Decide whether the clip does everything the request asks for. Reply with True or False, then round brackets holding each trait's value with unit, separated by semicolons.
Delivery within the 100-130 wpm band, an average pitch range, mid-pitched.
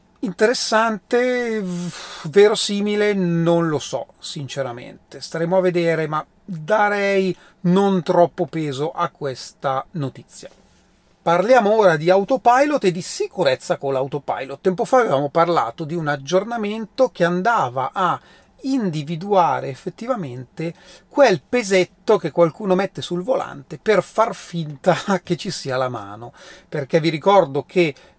True (120 wpm; 4.5 semitones; 180 Hz)